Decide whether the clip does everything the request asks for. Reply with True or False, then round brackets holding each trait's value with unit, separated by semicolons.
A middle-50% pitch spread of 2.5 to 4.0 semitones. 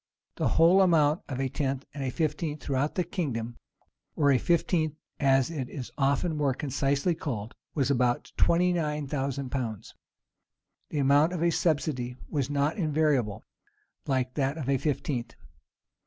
True (3.1 semitones)